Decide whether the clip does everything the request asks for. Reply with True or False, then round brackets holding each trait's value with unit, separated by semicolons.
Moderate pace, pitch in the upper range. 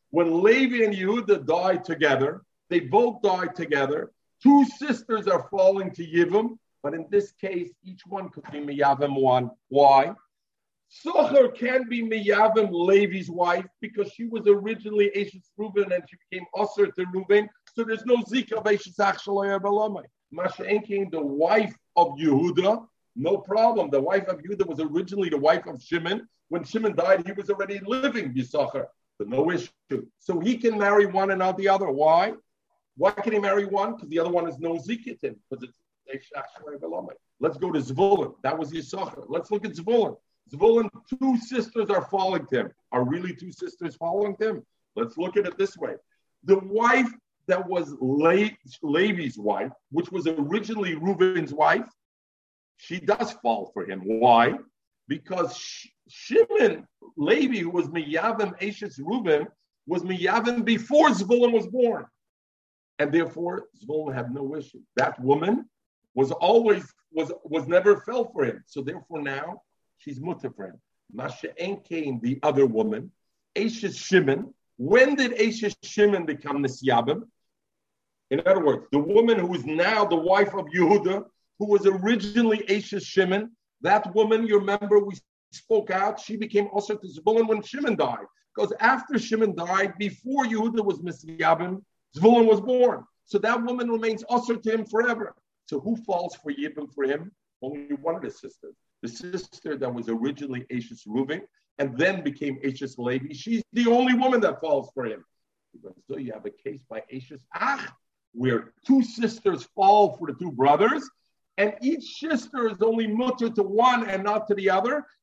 True (160 wpm; 200 Hz)